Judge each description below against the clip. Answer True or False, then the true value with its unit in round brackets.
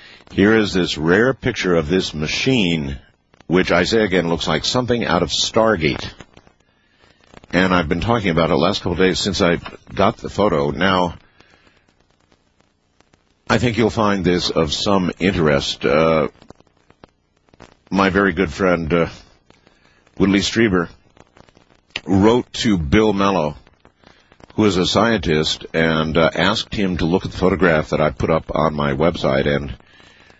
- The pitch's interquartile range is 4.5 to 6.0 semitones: False (3.9 semitones)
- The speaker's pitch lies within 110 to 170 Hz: False (90 Hz)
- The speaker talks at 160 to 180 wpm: False (150 wpm)